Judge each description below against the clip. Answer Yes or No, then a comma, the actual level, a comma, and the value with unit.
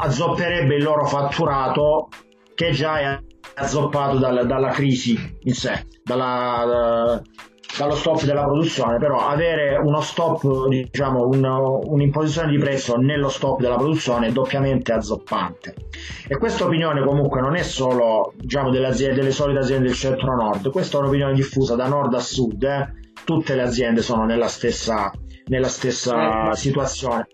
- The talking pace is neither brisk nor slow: Yes, average, 145 wpm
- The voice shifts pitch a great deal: No, average, 2.7 semitones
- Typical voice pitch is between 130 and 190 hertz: Yes, low, 135 Hz